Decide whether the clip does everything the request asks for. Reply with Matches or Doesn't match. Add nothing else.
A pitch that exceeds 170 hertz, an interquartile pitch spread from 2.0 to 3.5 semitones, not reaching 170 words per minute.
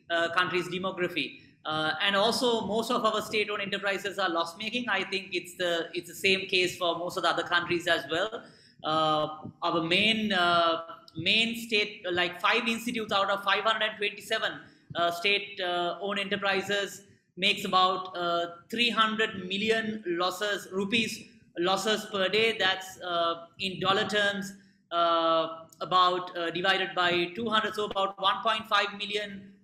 Matches